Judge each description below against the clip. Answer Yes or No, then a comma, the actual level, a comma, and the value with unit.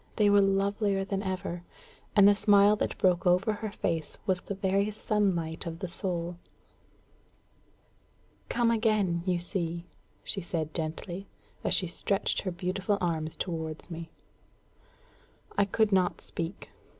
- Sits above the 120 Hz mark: Yes, high, 190 Hz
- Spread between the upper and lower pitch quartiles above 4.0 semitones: No, average, 2.9 semitones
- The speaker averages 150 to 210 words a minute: No, average, 140 wpm